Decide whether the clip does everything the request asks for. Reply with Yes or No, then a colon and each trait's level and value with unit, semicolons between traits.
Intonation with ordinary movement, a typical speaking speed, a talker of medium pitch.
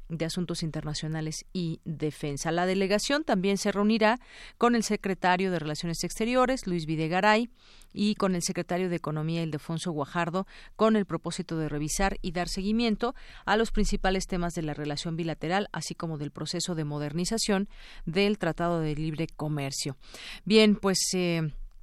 Yes: average, 4.0 semitones; average, 155 wpm; medium, 175 Hz